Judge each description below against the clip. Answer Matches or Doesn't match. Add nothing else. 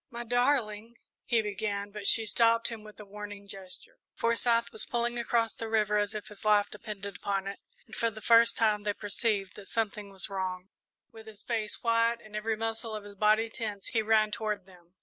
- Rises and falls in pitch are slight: Matches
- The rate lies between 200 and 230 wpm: Matches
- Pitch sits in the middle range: Doesn't match